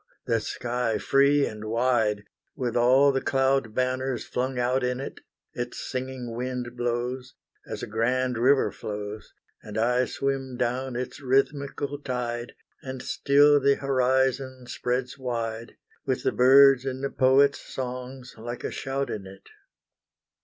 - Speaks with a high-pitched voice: No, low, 125 Hz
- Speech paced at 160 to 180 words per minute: No, average, 140 wpm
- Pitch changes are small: Yes, narrow, 1.8 semitones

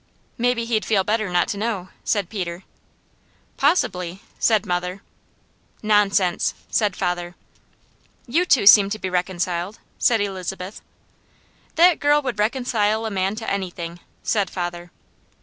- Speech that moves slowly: Yes, slow, 125 wpm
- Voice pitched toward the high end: Yes, high, 200 Hz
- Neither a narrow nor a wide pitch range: Yes, average, 3.6 semitones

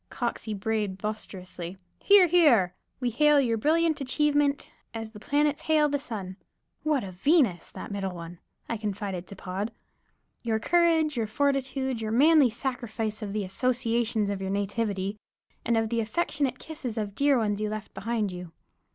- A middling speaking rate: Yes, average, 160 wpm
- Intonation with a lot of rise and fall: Yes, wide, 5.7 semitones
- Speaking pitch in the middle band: No, high, 225 Hz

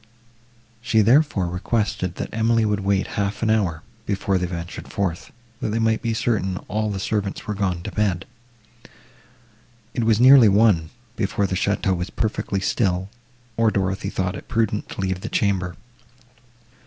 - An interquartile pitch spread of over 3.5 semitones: No, average, 3.0 semitones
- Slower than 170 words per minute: Yes, average, 160 wpm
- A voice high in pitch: No, low, 100 Hz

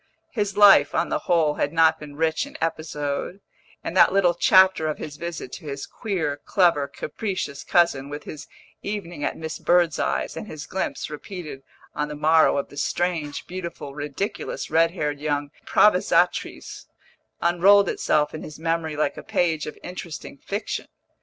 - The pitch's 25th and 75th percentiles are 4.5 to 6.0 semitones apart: No, average, 3.4 semitones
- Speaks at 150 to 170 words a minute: Yes, average, 160 wpm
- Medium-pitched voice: Yes, medium, 160 Hz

